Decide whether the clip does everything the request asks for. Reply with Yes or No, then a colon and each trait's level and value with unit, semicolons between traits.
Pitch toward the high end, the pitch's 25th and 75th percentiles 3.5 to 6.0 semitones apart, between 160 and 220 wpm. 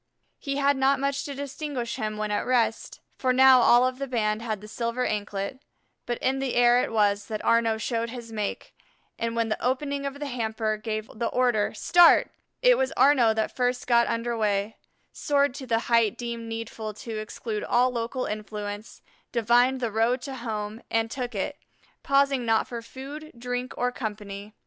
No: high, 235 Hz; average, 3.1 semitones; average, 185 wpm